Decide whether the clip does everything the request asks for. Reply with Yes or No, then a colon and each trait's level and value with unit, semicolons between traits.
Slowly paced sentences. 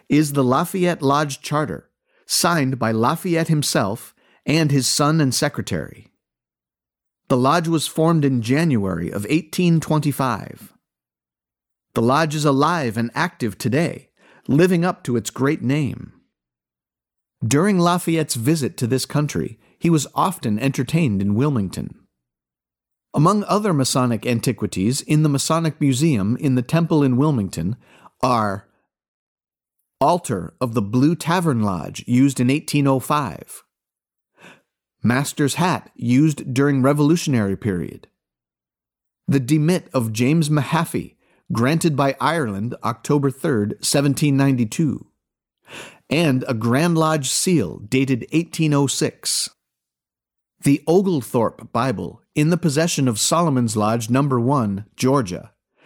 Yes: slow, 120 wpm